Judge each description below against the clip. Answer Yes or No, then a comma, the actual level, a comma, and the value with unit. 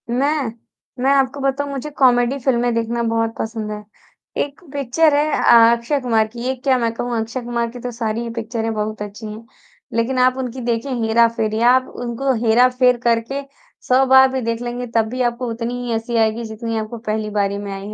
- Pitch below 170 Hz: No, high, 235 Hz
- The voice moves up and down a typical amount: No, narrow, 2.2 semitones